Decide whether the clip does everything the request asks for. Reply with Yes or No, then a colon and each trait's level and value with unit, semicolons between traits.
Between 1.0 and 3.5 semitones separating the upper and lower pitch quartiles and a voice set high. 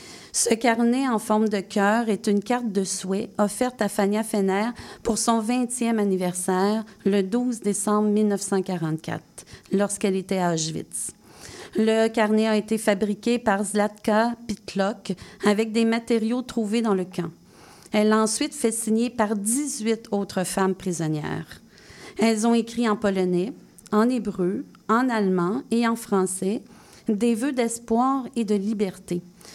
Yes: narrow, 2.6 semitones; high, 215 Hz